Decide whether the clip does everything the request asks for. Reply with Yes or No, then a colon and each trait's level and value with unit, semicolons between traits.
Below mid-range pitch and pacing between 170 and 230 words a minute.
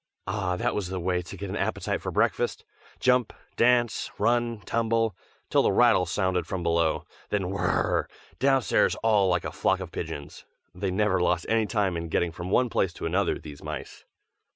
Yes: very low, 95 Hz; average, 180 wpm